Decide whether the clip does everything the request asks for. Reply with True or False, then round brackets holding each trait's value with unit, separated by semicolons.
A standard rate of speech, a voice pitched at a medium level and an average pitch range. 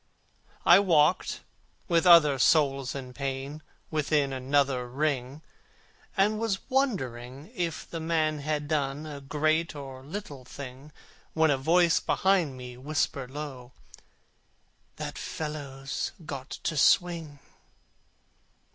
False (110 wpm; 145 Hz; 3.1 semitones)